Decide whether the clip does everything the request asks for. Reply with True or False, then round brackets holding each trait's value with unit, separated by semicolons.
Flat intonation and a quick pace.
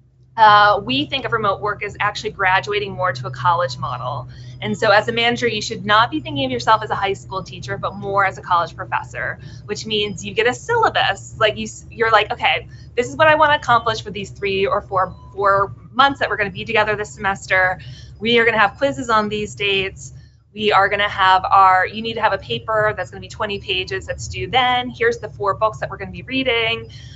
False (3.9 semitones; 245 wpm)